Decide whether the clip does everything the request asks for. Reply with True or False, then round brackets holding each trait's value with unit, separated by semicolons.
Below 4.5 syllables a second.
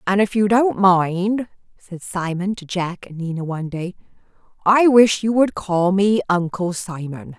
True (4.2 syllables/s)